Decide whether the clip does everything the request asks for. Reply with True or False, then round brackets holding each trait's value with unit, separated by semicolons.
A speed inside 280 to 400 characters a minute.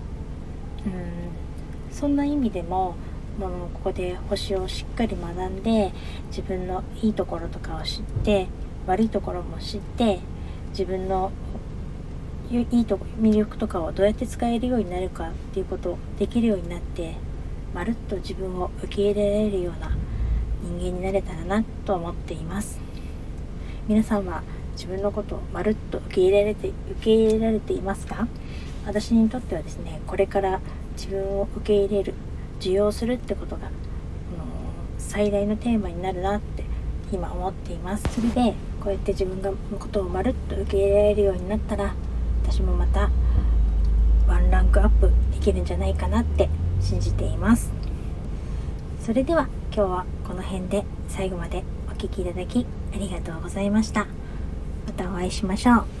True (330 characters per minute)